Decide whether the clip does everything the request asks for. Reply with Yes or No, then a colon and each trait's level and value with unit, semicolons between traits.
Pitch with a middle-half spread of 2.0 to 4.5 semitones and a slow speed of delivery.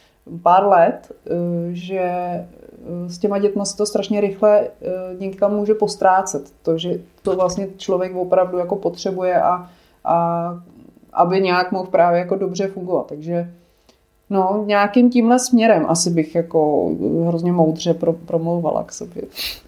No: narrow, 2.6 semitones; average, 130 wpm